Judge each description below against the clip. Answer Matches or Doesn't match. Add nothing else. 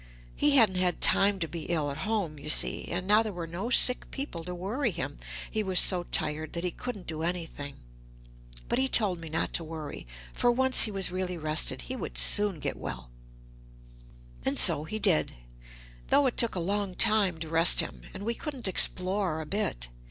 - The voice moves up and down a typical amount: Matches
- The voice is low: Doesn't match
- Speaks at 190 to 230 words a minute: Matches